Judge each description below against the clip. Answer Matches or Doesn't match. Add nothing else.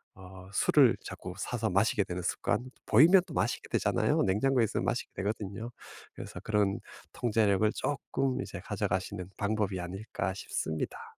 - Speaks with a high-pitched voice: Doesn't match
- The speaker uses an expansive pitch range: Doesn't match